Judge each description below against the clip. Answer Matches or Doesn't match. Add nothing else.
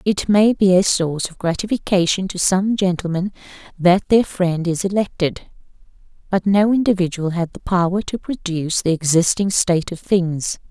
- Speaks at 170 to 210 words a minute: Doesn't match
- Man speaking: Doesn't match